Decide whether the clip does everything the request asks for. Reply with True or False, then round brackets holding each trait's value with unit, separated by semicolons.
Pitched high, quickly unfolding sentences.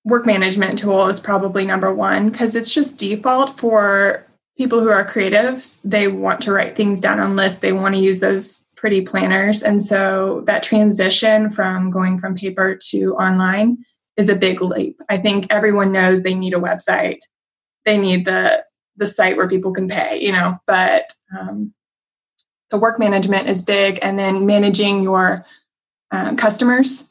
False (200 Hz; 170 wpm)